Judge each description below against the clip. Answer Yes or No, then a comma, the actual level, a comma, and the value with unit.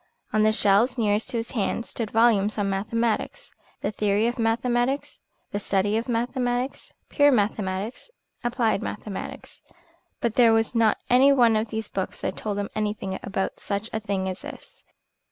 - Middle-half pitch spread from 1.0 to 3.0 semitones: Yes, average, 2.7 semitones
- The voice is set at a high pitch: Yes, high, 220 Hz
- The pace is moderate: Yes, average, 165 wpm